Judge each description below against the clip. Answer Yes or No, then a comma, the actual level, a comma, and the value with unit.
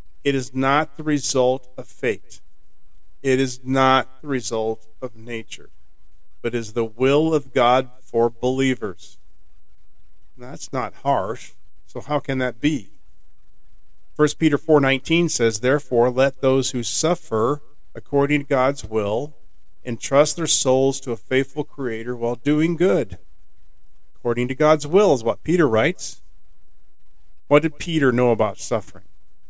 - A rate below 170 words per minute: Yes, average, 140 wpm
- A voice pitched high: No, low, 125 Hz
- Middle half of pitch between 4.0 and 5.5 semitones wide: Yes, average, 4.7 semitones